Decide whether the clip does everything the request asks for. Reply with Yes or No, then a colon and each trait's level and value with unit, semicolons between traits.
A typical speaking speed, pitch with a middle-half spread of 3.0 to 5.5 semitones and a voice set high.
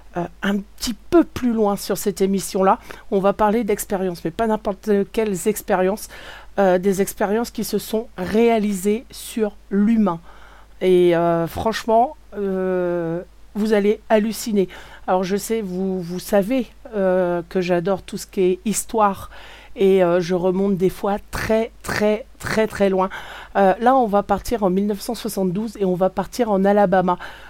No: average, 155 wpm; narrow, 2.6 semitones; high, 200 Hz